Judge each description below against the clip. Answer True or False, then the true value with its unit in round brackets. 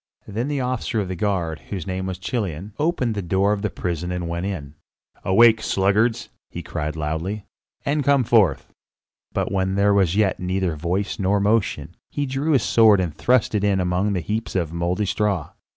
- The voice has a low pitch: True (95 Hz)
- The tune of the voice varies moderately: True (3.6 semitones)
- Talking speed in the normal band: True (190 wpm)